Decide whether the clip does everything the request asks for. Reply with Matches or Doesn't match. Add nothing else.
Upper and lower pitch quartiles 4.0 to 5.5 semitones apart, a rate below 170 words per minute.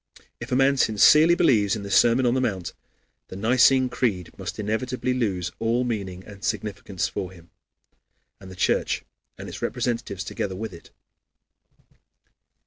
Matches